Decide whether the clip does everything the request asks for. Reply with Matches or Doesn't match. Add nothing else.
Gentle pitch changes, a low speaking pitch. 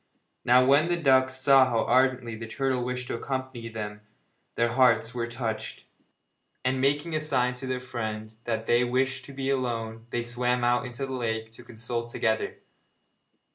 Matches